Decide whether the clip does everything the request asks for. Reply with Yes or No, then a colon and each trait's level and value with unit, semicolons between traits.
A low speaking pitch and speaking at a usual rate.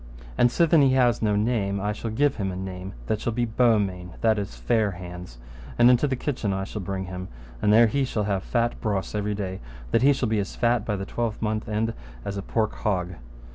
No: low, 105 Hz; fast, 225 wpm